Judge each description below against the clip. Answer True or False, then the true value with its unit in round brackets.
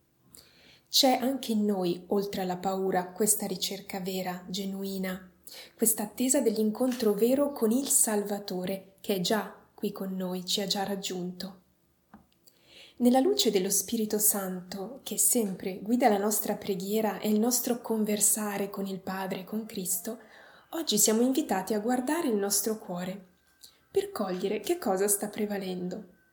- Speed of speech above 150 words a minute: False (145 wpm)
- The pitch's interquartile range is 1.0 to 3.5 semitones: True (2.6 semitones)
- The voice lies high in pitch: True (205 Hz)